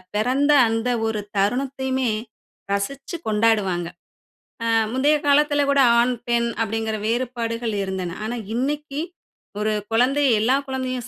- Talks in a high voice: Yes, high, 245 Hz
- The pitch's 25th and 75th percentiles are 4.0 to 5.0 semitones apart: No, average, 3.4 semitones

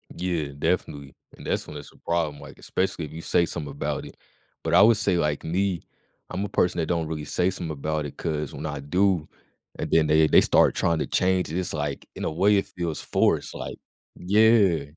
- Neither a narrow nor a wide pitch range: Yes, average, 3.3 semitones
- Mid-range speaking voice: No, very low, 80 Hz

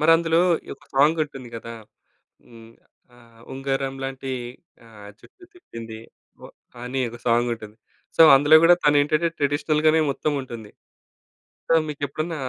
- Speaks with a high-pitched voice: No, low, 135 Hz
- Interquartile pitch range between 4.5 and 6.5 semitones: Yes, average, 4.8 semitones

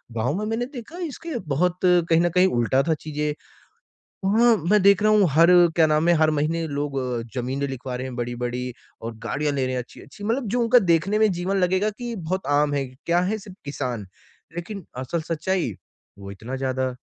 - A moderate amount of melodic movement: No, wide, 6.8 semitones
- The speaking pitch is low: No, medium, 165 Hz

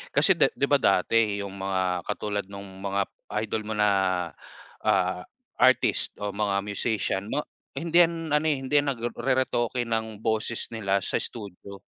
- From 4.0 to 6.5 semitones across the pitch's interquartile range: No, average, 3.3 semitones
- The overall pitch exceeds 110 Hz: No, low, 105 Hz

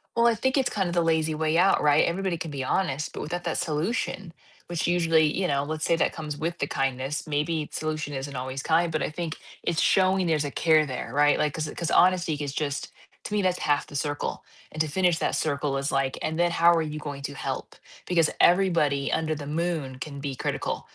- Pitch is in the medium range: Yes, medium, 155 Hz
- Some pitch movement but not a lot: Yes, average, 3.0 semitones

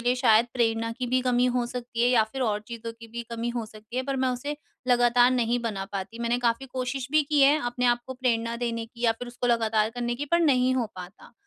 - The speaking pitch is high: Yes, high, 240 Hz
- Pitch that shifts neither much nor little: No, narrow, 1.6 semitones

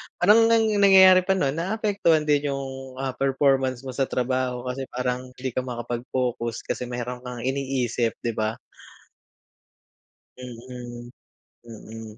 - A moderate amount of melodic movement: No, narrow, 2.3 semitones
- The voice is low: Yes, low, 130 Hz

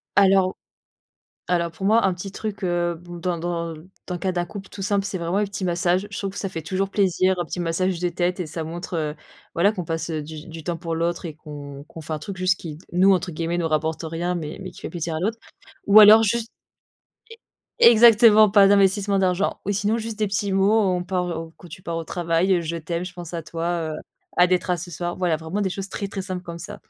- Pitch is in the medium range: Yes, medium, 180 Hz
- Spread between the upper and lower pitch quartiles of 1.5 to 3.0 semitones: Yes, average, 2.7 semitones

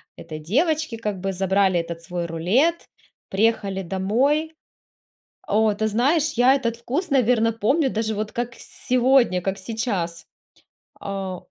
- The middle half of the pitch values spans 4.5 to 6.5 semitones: Yes, average, 4.9 semitones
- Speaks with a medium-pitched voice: No, high, 220 Hz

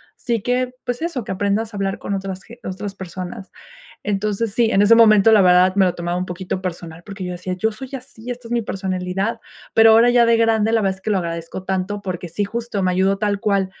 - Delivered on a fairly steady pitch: No, average, 3.3 semitones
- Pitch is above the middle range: Yes, high, 200 Hz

